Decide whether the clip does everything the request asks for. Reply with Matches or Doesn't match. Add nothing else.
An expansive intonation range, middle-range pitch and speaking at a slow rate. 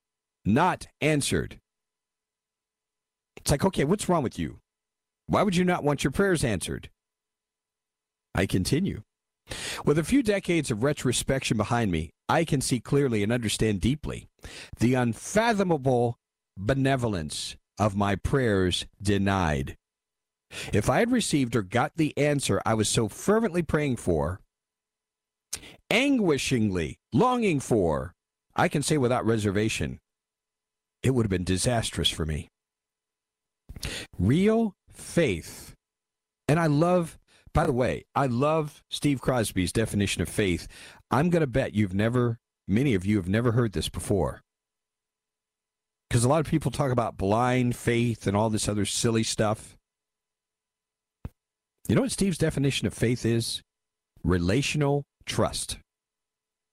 Doesn't match